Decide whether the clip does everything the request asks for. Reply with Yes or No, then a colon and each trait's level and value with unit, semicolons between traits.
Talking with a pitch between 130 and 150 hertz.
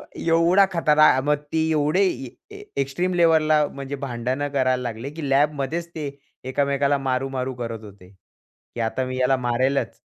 Yes: medium, 140 Hz